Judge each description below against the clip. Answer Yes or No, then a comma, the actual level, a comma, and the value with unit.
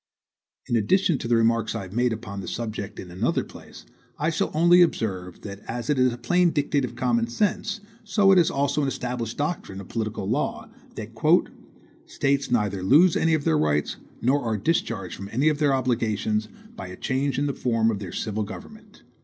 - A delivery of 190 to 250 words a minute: Yes, average, 200 wpm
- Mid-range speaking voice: No, low, 120 Hz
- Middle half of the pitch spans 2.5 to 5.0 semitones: No, wide, 5.5 semitones